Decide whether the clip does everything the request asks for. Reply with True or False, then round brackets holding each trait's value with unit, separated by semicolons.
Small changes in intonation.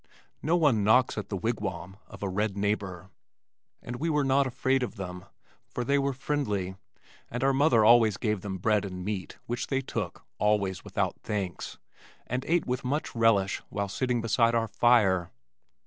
False (4.6 semitones)